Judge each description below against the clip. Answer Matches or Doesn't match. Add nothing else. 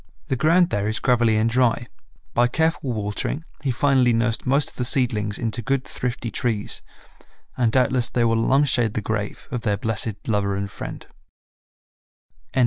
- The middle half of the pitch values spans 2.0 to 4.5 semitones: Matches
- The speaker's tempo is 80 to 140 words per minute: Doesn't match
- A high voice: Doesn't match